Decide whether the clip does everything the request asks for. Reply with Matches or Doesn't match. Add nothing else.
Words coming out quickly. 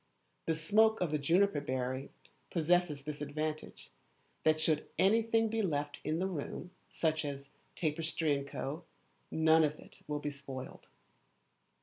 Doesn't match